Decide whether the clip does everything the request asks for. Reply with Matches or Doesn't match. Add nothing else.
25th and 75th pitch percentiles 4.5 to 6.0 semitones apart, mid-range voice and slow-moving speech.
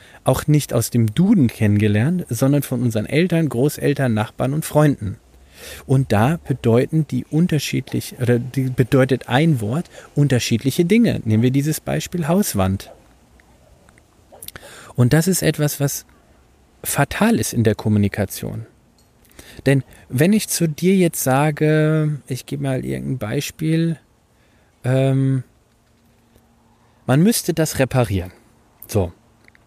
Doesn't match